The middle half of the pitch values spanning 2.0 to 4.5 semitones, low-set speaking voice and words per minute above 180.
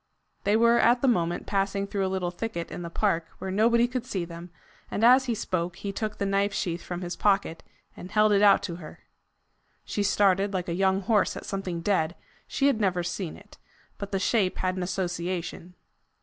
No: average, 2.9 semitones; high, 195 Hz; fast, 205 wpm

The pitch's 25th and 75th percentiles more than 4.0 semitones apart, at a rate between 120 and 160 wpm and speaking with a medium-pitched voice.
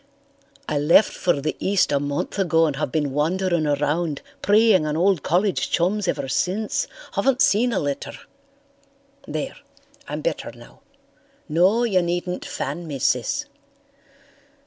Yes: average, 5.0 semitones; average, 140 wpm; medium, 175 Hz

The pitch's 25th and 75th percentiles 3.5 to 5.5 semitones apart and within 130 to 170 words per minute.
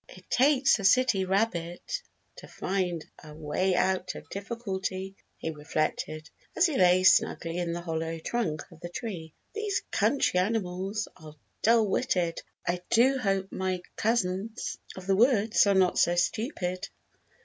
Yes: average, 4.3 semitones; average, 150 wpm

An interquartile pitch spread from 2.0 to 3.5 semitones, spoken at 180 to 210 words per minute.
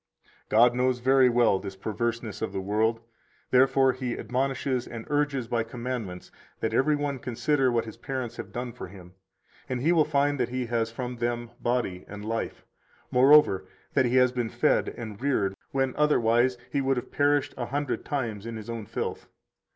Yes: average, 2.8 semitones; average, 185 wpm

